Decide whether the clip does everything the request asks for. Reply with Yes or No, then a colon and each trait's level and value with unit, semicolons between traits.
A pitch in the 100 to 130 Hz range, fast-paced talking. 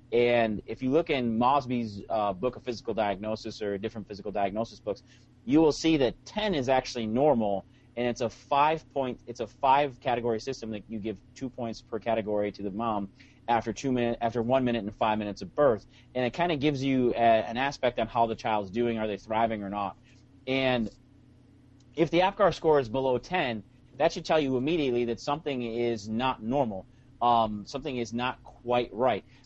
No: low, 120 Hz; average, 195 wpm